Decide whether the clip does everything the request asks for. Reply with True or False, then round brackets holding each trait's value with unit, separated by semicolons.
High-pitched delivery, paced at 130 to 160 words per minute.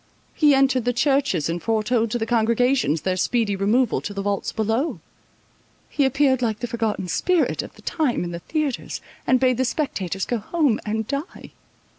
False (235 Hz; 180 wpm)